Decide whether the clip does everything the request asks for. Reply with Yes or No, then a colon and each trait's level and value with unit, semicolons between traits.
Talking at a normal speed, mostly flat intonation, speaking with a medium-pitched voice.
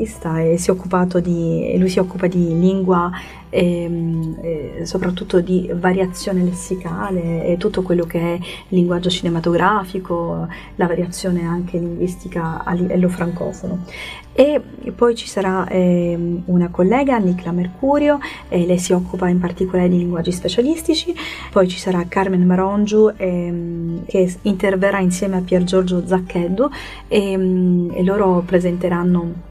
Yes: average, 130 wpm; narrow, 1.6 semitones; medium, 180 Hz